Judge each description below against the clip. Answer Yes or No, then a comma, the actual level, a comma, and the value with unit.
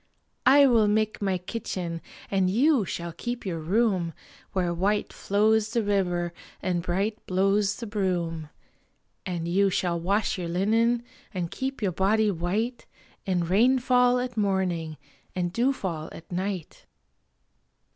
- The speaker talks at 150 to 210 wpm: No, slow, 135 wpm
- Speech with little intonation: No, average, 3.9 semitones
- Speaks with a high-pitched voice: Yes, high, 195 Hz